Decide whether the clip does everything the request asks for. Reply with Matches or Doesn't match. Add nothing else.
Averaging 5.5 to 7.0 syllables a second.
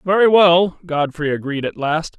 Doesn't match